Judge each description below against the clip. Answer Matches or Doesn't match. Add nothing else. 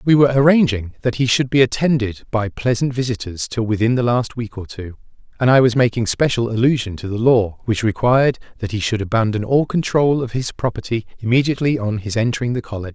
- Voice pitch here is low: Matches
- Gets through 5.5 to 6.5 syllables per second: Matches